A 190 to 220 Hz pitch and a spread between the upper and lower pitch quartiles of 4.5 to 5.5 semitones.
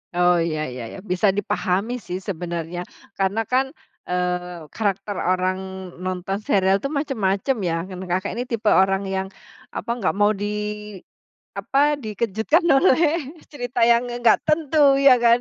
Yes: high, 200 Hz; average, 5.1 semitones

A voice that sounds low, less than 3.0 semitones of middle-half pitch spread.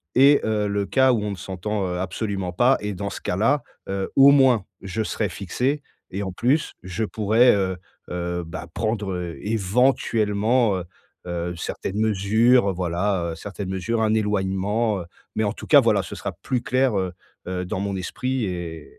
No: low, 100 Hz; average, 3.5 semitones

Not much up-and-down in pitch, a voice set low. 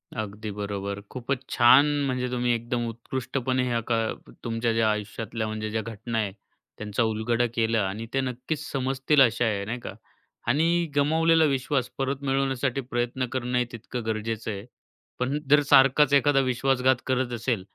No: average, 3.0 semitones; low, 120 Hz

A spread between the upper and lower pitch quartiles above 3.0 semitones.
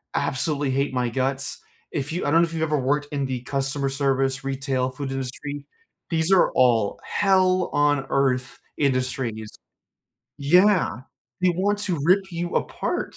Yes: average, 3.9 semitones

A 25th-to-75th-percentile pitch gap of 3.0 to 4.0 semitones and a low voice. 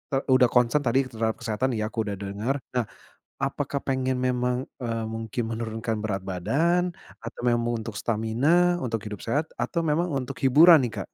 Yes: average, 3.4 semitones; low, 120 Hz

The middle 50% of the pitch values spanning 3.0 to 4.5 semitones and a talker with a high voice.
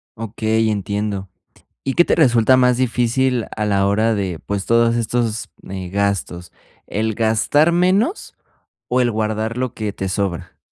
No: average, 3.3 semitones; low, 110 Hz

